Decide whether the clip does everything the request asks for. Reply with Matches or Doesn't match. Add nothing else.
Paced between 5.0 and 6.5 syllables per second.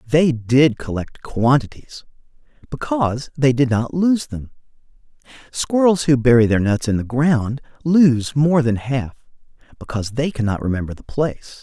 Doesn't match